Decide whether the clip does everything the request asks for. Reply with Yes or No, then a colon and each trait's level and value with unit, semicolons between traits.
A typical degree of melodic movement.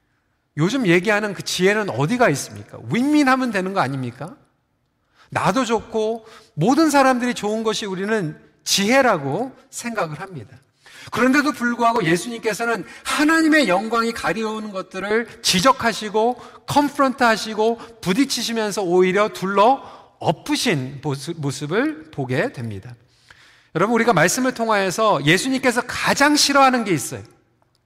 No: wide, 6.8 semitones